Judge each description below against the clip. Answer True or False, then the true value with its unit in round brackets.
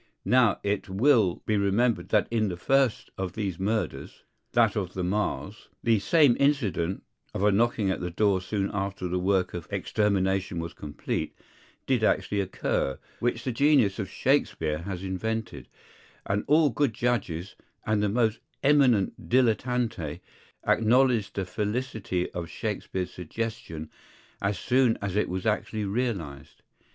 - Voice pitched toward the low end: True (105 Hz)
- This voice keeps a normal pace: True (145 wpm)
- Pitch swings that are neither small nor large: True (4.2 semitones)